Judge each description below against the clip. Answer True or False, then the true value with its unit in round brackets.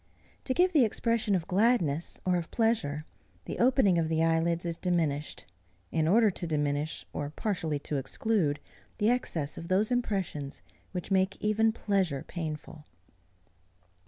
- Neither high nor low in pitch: True (175 Hz)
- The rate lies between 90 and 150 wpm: True (145 wpm)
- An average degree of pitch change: False (5.7 semitones)